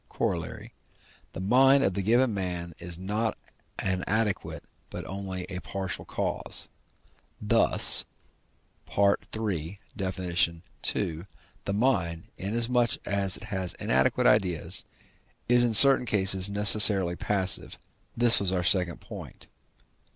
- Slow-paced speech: Yes, slow, 115 wpm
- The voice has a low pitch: Yes, low, 100 Hz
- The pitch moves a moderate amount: Yes, average, 3.1 semitones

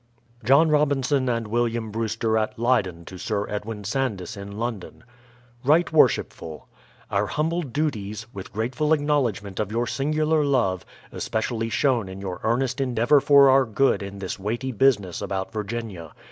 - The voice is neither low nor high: No, low, 115 Hz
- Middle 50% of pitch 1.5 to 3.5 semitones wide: No, average, 5.0 semitones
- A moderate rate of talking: Yes, average, 150 wpm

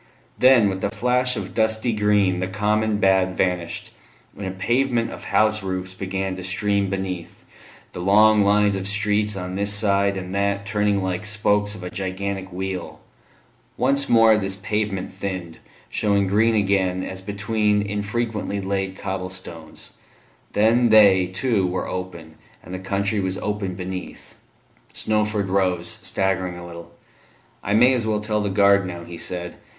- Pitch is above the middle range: No, low, 100 Hz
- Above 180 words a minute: No, average, 155 wpm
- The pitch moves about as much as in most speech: No, narrow, 2.1 semitones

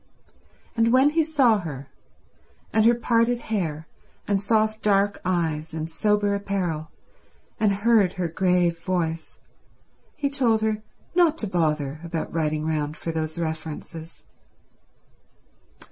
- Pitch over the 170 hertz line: Yes, medium, 185 Hz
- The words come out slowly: Yes, slow, 125 wpm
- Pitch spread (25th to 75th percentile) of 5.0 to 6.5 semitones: Yes, wide, 5.5 semitones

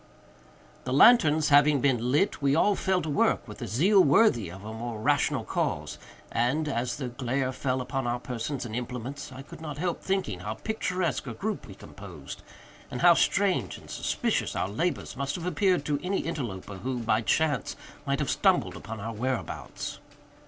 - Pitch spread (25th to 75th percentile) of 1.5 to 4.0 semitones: No, average, 5.2 semitones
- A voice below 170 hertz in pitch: Yes, low, 135 Hz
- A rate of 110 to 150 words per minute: No, average, 180 wpm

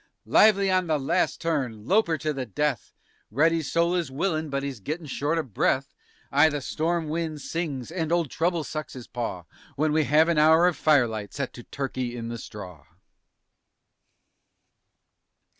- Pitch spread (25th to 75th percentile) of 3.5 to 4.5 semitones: Yes, average, 4.1 semitones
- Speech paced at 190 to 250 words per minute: No, average, 170 wpm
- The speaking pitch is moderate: Yes, medium, 150 Hz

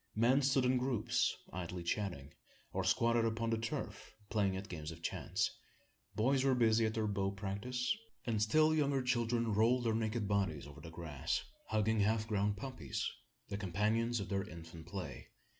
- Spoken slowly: No, average, 170 wpm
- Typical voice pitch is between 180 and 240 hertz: No, low, 110 Hz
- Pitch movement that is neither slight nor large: Yes, average, 3.4 semitones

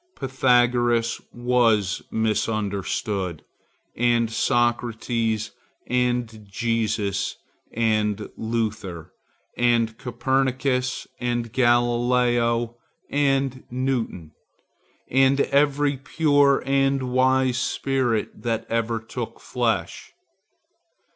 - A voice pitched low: Yes, low, 120 Hz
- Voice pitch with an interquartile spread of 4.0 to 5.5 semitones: No, narrow, 2.6 semitones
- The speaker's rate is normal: No, slow, 70 wpm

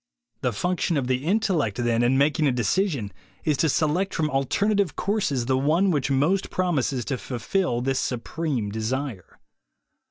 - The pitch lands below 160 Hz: Yes, medium, 140 Hz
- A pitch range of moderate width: No, wide, 5.9 semitones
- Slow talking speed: No, average, 155 wpm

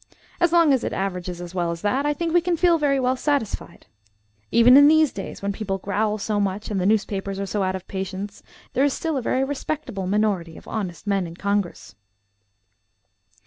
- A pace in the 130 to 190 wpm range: No, fast, 205 wpm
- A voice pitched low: No, high, 210 Hz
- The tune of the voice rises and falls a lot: Yes, wide, 6.3 semitones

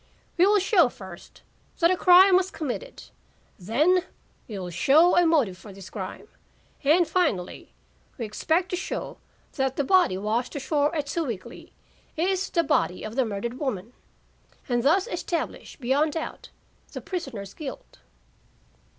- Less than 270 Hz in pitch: No, very high, 285 Hz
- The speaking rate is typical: Yes, average, 145 wpm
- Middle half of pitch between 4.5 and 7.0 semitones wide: No, wide, 8.1 semitones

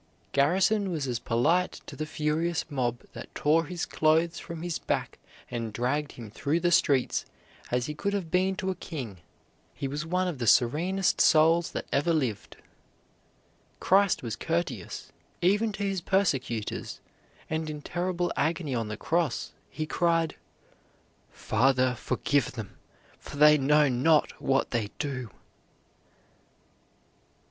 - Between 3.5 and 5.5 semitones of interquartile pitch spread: Yes, average, 5.2 semitones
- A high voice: No, medium, 155 Hz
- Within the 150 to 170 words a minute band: No, average, 140 wpm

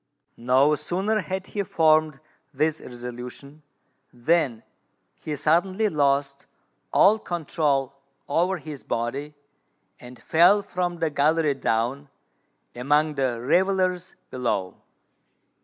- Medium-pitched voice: Yes, medium, 150 Hz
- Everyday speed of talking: No, slow, 100 wpm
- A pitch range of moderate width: Yes, average, 4.4 semitones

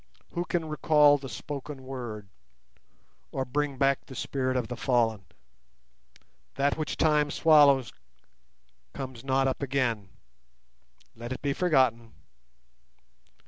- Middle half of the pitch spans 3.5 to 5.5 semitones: No, average, 2.9 semitones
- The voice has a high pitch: No, low, 135 Hz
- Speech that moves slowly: Yes, slow, 115 wpm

